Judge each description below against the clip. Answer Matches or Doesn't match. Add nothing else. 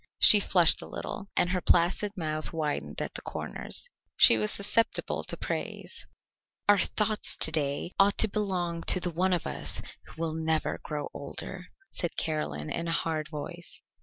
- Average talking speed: Matches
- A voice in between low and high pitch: Matches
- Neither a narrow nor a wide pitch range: Matches